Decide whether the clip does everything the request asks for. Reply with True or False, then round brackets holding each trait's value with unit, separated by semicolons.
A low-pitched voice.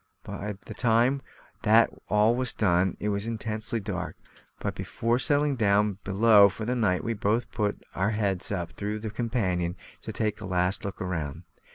True (105 Hz)